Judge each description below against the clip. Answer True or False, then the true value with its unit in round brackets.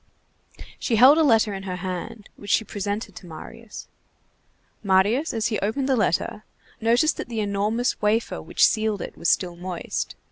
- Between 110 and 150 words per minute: False (170 wpm)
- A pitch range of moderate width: True (3.2 semitones)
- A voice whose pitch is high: True (215 Hz)